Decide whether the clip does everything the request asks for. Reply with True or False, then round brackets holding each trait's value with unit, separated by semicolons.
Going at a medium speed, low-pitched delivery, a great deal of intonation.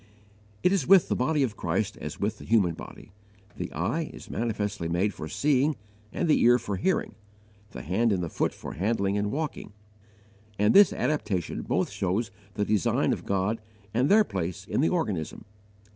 True (175 wpm; 105 Hz; 6.7 semitones)